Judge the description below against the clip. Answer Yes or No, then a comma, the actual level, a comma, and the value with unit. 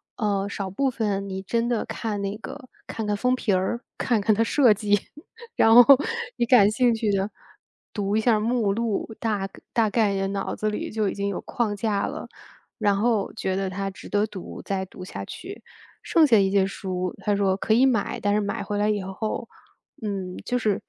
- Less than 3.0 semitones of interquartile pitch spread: Yes, narrow, 2.5 semitones